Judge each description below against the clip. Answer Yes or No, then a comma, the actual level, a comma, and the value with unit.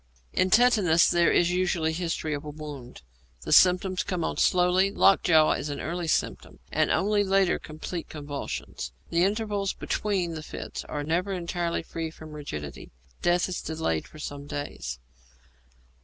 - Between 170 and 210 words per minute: No, average, 155 wpm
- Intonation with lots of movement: No, average, 3.4 semitones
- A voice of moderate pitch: Yes, medium, 170 Hz